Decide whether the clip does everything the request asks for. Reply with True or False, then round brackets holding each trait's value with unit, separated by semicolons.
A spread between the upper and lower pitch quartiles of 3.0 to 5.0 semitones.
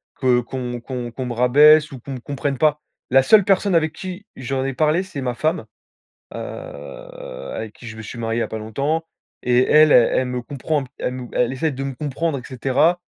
True (4.1 semitones)